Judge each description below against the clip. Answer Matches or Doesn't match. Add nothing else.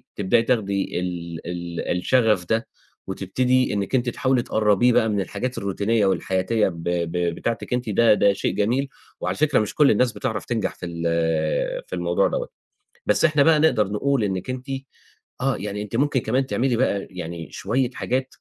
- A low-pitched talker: Matches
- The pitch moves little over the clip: Doesn't match